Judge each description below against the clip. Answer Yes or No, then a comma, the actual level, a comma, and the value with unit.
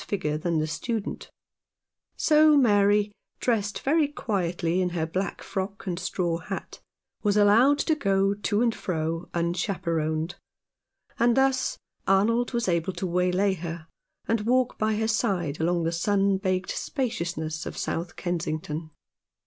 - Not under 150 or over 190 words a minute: No, average, 140 wpm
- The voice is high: Yes, high, 195 Hz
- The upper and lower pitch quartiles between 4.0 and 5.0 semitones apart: Yes, average, 4.5 semitones